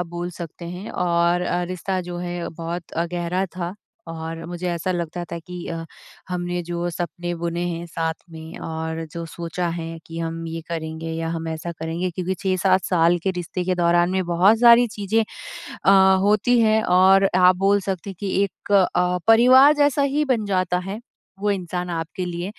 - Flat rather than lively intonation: Yes, narrow, 2.1 semitones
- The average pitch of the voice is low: No, medium, 175 Hz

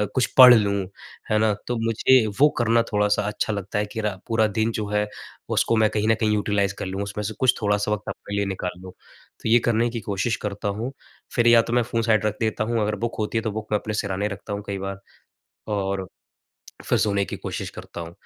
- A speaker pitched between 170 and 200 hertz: No, low, 105 Hz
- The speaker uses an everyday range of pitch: No, narrow, 2.0 semitones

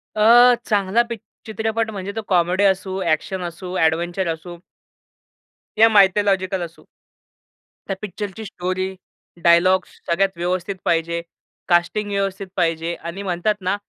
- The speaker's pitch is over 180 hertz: Yes, high, 190 Hz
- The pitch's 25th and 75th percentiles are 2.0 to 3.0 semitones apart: Yes, average, 2.7 semitones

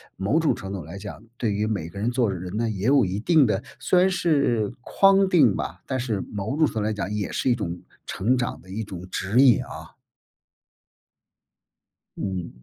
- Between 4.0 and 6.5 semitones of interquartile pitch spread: Yes, average, 5.2 semitones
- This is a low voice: Yes, low, 110 Hz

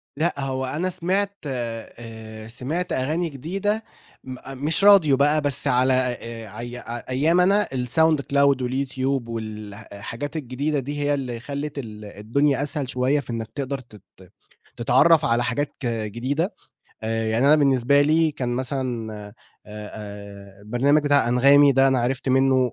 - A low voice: Yes, low, 130 Hz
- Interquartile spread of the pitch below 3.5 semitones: No, average, 3.8 semitones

